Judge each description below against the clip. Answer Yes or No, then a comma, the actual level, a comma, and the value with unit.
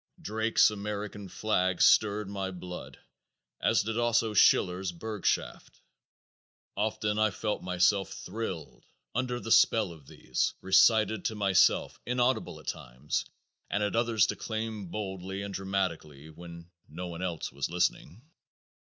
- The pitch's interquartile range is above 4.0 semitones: No, average, 3.3 semitones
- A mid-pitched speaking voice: No, low, 100 Hz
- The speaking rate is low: Yes, slow, 125 wpm